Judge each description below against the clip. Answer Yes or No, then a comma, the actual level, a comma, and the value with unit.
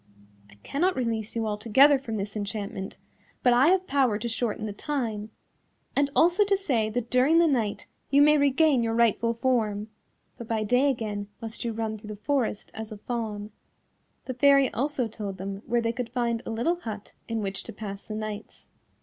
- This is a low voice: No, high, 230 Hz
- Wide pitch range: No, average, 3.9 semitones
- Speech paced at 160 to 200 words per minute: Yes, average, 190 wpm